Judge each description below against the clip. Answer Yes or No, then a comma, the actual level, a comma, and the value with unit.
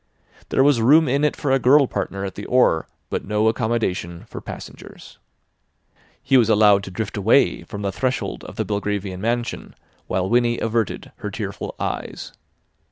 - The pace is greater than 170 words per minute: No, average, 165 wpm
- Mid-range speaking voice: No, low, 110 Hz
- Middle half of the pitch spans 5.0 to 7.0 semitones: No, average, 4.1 semitones